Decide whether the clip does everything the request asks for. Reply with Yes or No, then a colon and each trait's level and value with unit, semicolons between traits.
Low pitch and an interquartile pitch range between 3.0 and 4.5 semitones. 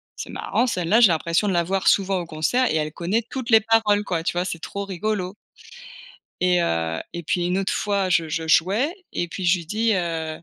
No: medium, 180 Hz; average, 3.7 semitones